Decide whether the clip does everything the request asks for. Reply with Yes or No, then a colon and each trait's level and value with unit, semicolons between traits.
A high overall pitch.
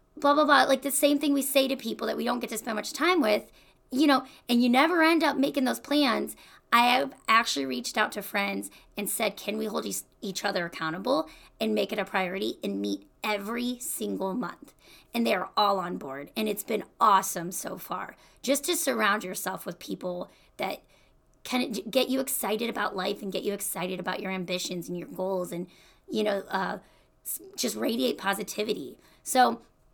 Yes: high, 215 Hz